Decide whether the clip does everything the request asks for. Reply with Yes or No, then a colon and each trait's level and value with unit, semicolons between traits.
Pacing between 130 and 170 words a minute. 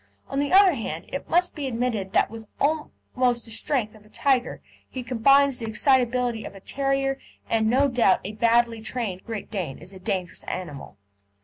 No: average, 190 wpm